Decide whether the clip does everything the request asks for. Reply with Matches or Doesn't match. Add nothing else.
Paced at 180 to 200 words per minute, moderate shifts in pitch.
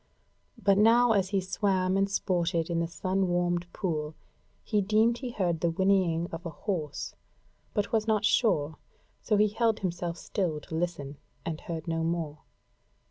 Doesn't match